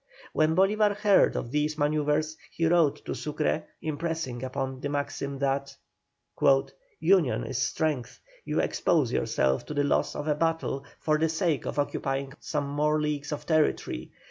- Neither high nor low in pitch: Yes, medium, 150 Hz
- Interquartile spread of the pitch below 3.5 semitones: Yes, narrow, 2.4 semitones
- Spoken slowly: No, average, 160 wpm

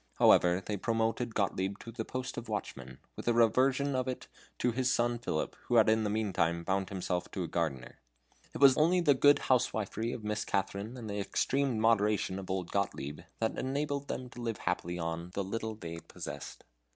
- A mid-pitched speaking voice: No, low, 110 Hz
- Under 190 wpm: No, average, 195 wpm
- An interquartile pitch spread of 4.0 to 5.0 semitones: Yes, average, 4.7 semitones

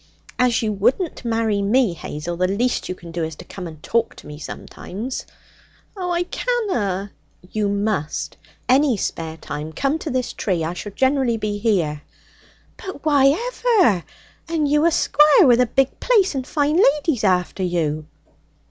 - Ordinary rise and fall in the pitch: No, wide, 7.9 semitones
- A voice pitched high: Yes, high, 225 Hz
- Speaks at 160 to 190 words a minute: Yes, average, 165 wpm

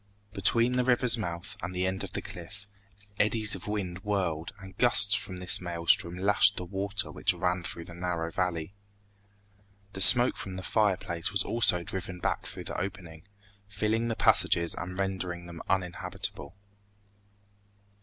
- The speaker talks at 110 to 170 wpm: Yes, average, 155 wpm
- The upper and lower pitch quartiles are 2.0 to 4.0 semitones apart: Yes, average, 2.8 semitones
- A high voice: No, very low, 95 Hz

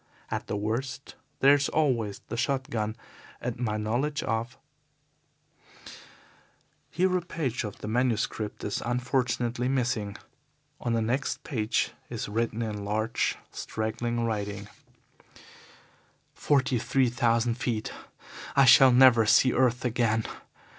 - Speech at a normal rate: No, slow, 125 wpm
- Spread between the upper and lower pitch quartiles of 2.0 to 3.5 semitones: Yes, average, 2.9 semitones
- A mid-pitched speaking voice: No, low, 120 Hz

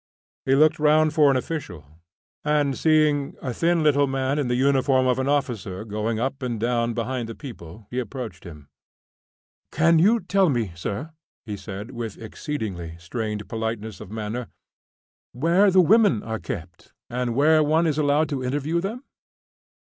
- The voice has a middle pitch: No, low, 130 Hz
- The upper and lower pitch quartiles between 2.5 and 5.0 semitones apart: No, wide, 5.4 semitones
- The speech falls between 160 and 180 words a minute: Yes, average, 165 wpm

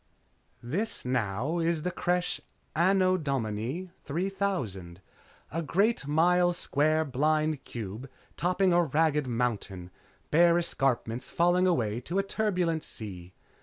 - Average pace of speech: No, slow, 120 wpm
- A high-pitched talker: No, medium, 155 Hz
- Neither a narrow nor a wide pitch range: No, wide, 6.4 semitones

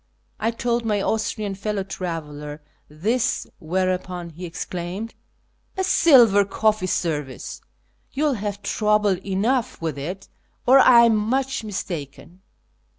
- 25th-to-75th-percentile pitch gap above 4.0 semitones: Yes, average, 4.6 semitones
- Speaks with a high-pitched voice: Yes, high, 200 Hz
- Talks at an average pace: No, slow, 125 wpm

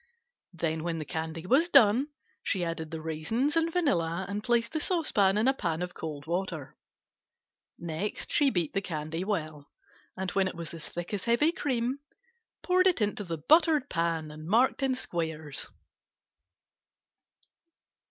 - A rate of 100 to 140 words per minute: No, average, 155 wpm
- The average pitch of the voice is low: No, medium, 185 Hz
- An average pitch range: No, wide, 7.9 semitones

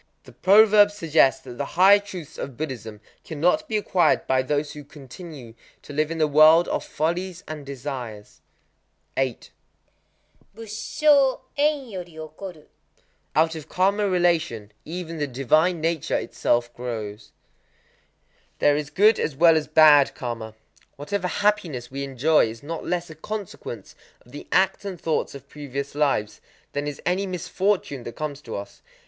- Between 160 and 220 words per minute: No, average, 150 wpm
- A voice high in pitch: No, medium, 155 Hz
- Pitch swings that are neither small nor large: Yes, average, 5.0 semitones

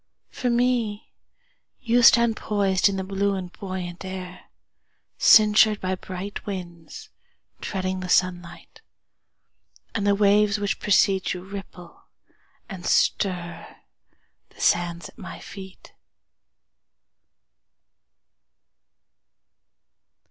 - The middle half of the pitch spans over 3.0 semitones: No, narrow, 2.4 semitones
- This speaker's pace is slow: Yes, slow, 75 wpm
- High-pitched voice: Yes, high, 195 Hz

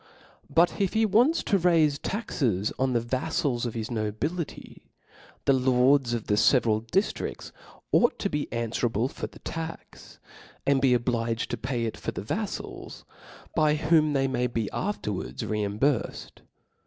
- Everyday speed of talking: Yes, average, 160 wpm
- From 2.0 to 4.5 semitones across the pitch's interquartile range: No, average, 5.1 semitones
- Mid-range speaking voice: No, low, 130 Hz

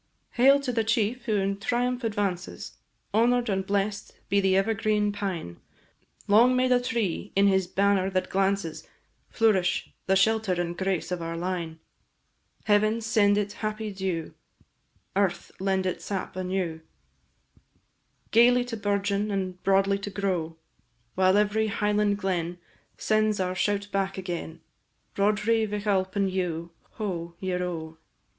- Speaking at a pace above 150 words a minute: No, slow, 135 wpm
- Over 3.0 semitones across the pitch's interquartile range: No, narrow, 2.5 semitones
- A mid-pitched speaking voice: No, high, 200 Hz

